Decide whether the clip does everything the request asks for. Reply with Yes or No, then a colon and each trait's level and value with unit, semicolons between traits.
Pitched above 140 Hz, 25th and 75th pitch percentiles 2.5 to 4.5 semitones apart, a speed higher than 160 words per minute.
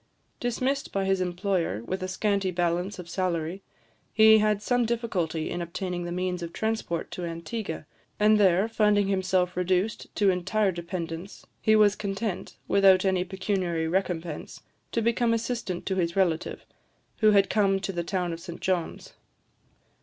No: high, 190 Hz; average, 3.1 semitones; average, 155 wpm